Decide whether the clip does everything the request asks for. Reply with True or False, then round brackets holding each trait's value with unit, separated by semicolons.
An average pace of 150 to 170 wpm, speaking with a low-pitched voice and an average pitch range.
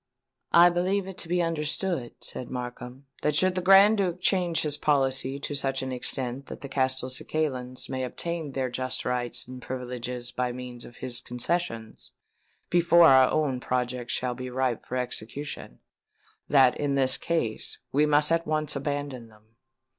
True (155 wpm; 130 Hz; 4.0 semitones)